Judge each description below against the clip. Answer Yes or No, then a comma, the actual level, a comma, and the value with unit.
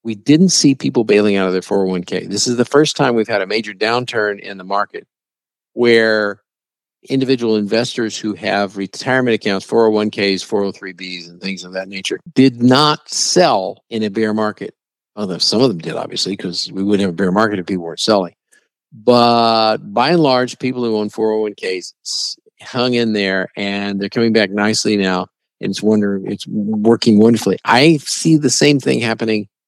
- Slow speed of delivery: No, average, 180 wpm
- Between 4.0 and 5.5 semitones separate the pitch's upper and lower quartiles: No, average, 3.3 semitones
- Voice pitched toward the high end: No, low, 110 Hz